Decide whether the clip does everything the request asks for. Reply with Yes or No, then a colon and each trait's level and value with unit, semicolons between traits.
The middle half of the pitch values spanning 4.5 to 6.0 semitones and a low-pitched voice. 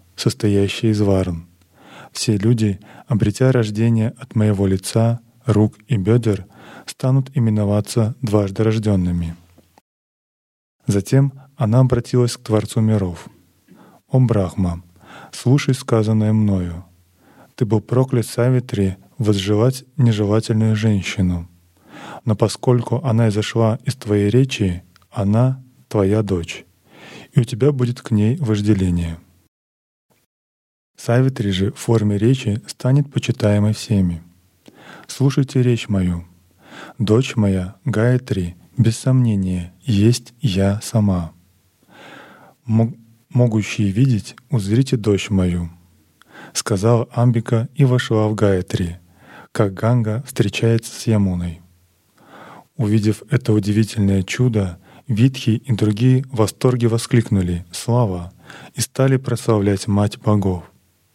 No: average, 4.0 semitones; low, 110 Hz